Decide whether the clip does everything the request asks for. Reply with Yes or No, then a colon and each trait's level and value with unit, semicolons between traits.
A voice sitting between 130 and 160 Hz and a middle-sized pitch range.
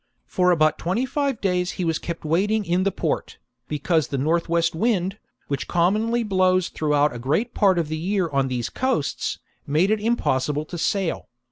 No: medium, 175 Hz; average, 4.6 semitones